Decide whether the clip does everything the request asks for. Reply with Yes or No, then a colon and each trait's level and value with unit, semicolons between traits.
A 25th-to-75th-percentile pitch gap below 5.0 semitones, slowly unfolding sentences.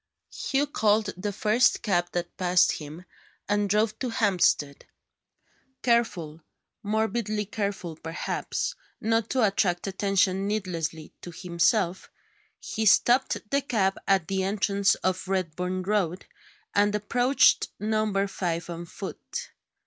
Yes: average, 3.3 semitones; slow, 120 wpm